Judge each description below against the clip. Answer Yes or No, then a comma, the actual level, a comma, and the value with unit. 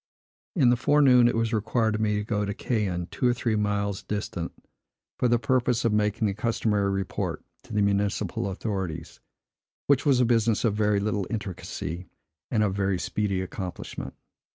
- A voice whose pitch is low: Yes, low, 105 Hz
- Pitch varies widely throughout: No, average, 2.8 semitones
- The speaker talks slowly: No, average, 175 wpm